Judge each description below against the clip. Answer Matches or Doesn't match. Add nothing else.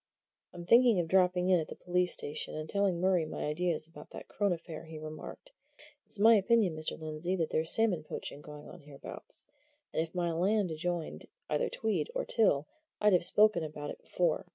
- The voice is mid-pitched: Matches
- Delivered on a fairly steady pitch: Doesn't match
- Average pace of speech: Matches